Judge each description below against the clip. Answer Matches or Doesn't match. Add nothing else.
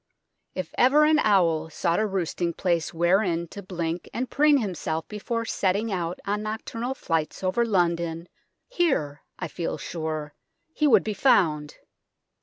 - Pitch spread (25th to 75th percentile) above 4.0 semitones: Matches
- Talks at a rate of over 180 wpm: Doesn't match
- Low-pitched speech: Doesn't match